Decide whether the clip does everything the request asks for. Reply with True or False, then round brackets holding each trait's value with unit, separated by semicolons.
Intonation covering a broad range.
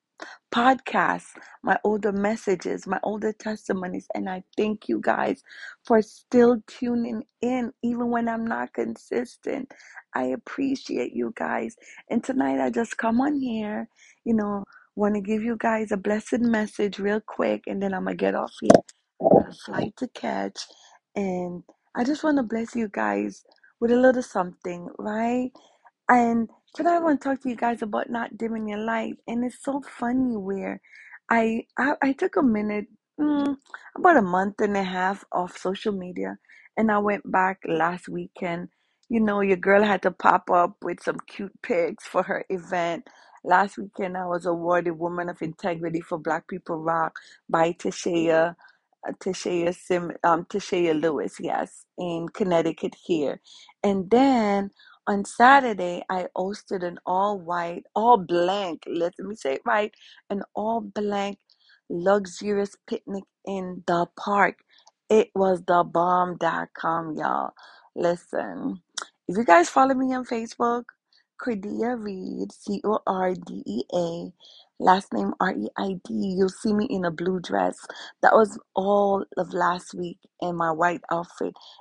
False (4.7 semitones)